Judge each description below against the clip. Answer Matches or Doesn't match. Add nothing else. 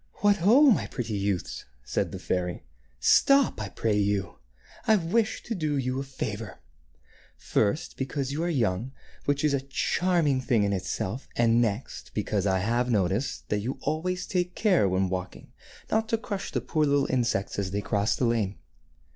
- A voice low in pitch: Matches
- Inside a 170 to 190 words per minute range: Matches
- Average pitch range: Doesn't match